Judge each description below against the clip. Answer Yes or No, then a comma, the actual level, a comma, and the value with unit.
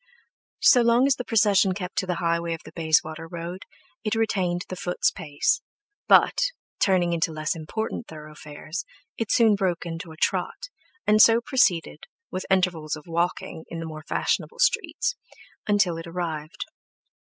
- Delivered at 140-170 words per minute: Yes, average, 160 wpm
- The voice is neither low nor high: Yes, medium, 175 Hz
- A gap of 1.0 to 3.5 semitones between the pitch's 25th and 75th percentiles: No, average, 4.1 semitones